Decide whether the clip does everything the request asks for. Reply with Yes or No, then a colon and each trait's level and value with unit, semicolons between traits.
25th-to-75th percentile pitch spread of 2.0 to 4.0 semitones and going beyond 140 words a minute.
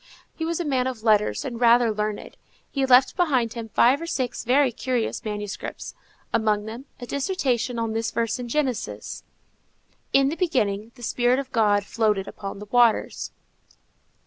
Yes: average, 3.3 semitones; average, 165 wpm